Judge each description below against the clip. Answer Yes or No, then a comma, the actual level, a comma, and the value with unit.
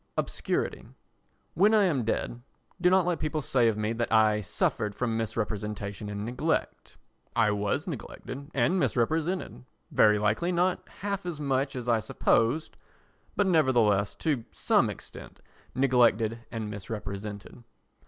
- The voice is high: No, low, 120 Hz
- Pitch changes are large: Yes, wide, 6.5 semitones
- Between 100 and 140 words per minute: Yes, slow, 135 wpm